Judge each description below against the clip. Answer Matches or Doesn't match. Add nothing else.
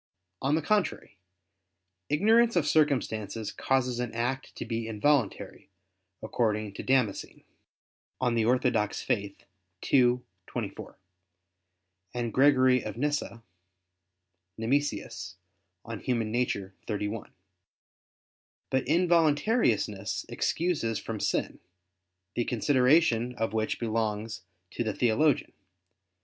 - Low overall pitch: Matches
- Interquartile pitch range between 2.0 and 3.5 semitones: Doesn't match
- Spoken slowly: Matches